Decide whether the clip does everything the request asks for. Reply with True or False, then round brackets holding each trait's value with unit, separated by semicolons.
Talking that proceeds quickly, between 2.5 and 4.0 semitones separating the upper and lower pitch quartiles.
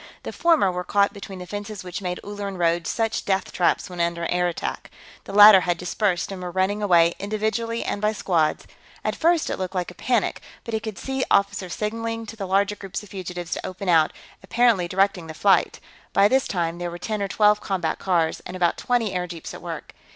True (215 wpm; 2.9 semitones)